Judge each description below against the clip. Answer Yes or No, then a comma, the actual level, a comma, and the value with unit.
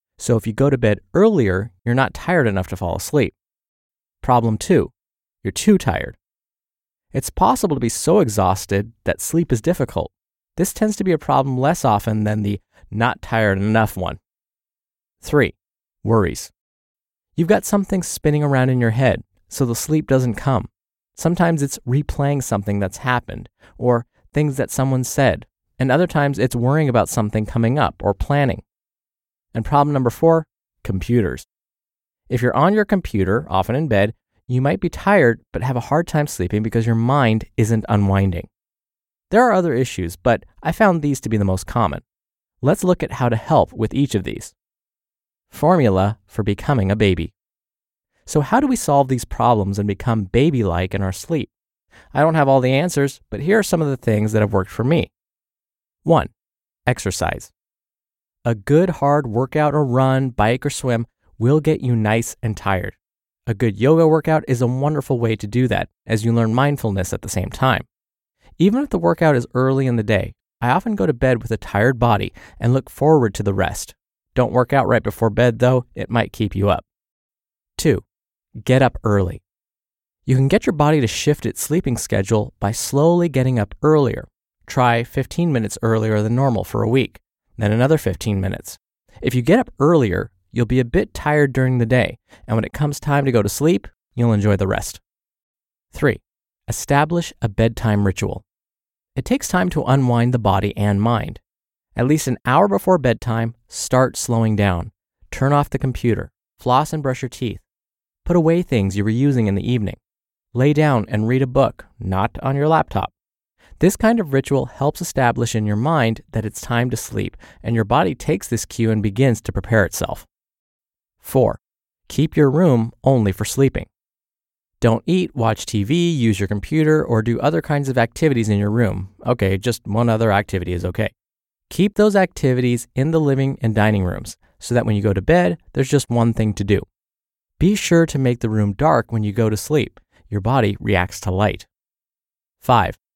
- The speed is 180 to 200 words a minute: Yes, average, 185 wpm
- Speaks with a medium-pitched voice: No, low, 120 Hz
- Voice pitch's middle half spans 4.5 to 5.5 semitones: Yes, average, 5.2 semitones